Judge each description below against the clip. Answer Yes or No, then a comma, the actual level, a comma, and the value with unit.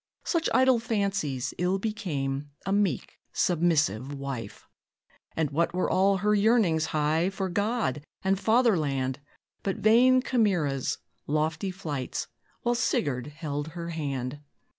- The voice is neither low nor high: Yes, medium, 170 Hz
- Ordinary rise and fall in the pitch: No, wide, 6.0 semitones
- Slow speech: Yes, slow, 120 wpm